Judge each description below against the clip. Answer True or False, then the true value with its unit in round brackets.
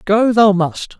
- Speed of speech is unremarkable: True (180 wpm)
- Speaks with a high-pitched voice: True (200 Hz)